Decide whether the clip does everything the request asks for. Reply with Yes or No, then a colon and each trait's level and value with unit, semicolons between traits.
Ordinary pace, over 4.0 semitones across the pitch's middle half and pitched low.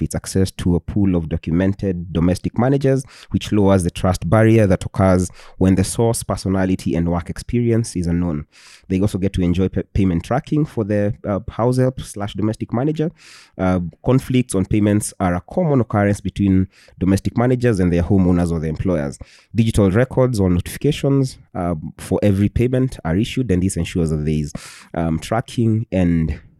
Yes: average, 175 wpm; average, 4.5 semitones; very low, 95 Hz